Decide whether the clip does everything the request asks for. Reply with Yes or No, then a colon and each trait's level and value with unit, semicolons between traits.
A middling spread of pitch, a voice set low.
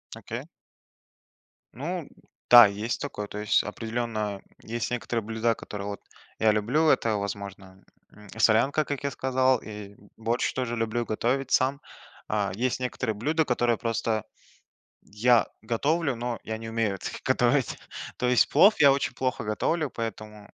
Yes: average, 3.3 semitones; low, 115 Hz